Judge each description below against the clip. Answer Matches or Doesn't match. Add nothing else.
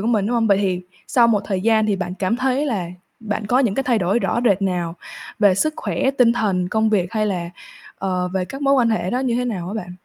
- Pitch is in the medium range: Doesn't match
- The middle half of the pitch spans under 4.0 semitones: Doesn't match